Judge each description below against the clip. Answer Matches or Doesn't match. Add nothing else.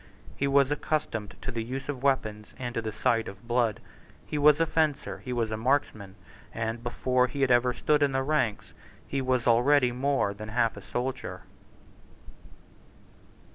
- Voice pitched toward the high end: Doesn't match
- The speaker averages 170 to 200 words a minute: Matches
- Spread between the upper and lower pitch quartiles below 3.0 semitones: Doesn't match